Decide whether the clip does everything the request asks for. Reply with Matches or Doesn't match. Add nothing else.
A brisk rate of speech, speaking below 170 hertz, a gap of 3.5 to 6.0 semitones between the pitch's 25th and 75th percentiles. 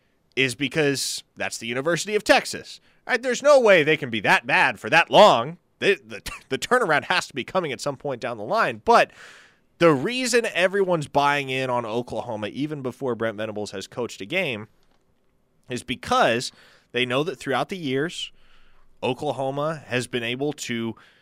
Doesn't match